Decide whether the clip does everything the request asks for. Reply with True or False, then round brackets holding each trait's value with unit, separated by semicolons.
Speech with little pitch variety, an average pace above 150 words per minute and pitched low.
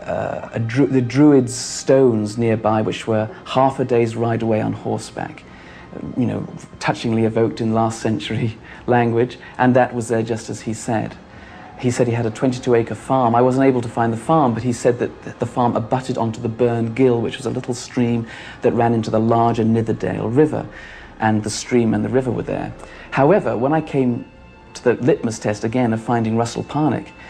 True (2.1 semitones; 205 wpm; 115 Hz)